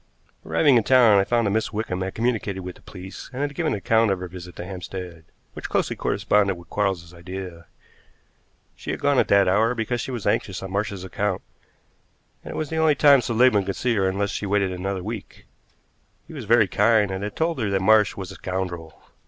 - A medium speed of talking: No, fast, 220 wpm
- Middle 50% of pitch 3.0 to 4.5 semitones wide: Yes, average, 3.5 semitones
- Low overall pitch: Yes, low, 100 Hz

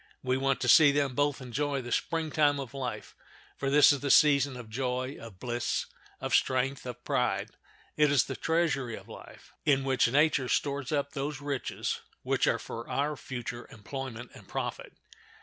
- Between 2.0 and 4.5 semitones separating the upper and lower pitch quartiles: Yes, narrow, 2.5 semitones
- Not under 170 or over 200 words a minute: Yes, average, 180 wpm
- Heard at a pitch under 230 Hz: Yes, low, 135 Hz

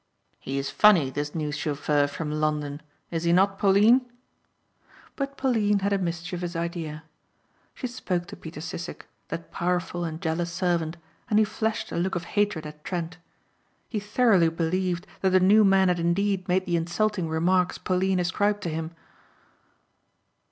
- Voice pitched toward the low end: No, medium, 175 Hz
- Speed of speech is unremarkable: Yes, average, 160 wpm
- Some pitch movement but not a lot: Yes, average, 3.4 semitones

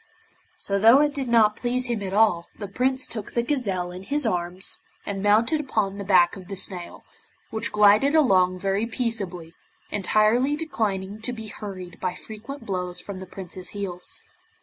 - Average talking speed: Yes, average, 170 wpm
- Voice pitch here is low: No, high, 205 Hz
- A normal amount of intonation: Yes, average, 4.0 semitones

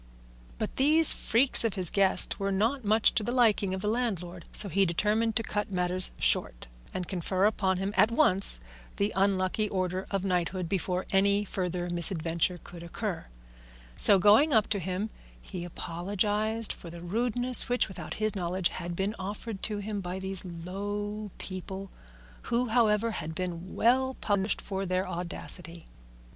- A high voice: Yes, high, 195 Hz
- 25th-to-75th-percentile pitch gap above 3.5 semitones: No, average, 2.9 semitones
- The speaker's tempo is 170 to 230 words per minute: No, average, 160 wpm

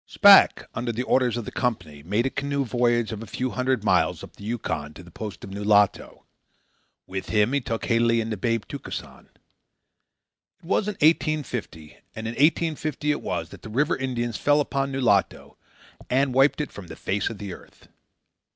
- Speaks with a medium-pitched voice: No, low, 120 Hz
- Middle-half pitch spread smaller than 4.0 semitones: No, average, 4.7 semitones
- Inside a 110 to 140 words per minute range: No, average, 190 wpm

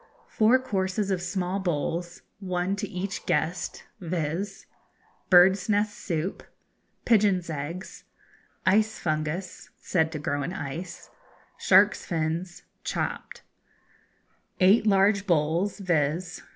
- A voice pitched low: No, medium, 180 Hz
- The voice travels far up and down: No, average, 3.1 semitones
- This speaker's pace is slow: Yes, slow, 105 wpm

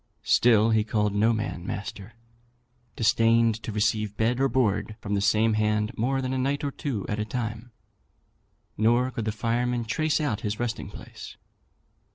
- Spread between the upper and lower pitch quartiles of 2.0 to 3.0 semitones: Yes, narrow, 2.5 semitones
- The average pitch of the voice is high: No, low, 115 Hz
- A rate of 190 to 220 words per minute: No, average, 170 wpm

